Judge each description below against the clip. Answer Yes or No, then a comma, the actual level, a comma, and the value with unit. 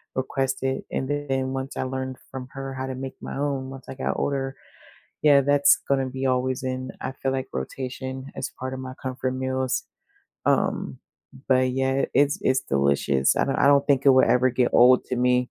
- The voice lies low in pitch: Yes, low, 130 Hz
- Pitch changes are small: Yes, narrow, 0.7 semitones